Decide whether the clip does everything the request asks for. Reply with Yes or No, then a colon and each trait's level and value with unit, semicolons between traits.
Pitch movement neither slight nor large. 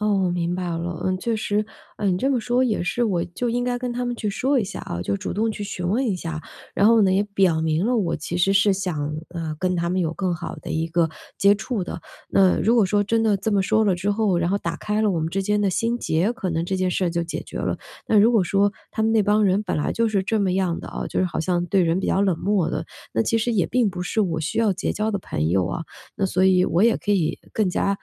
Yes: average, 3.6 semitones